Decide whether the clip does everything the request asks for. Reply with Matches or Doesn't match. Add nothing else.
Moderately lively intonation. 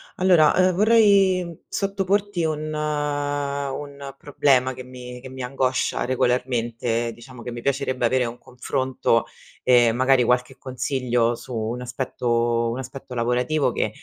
Matches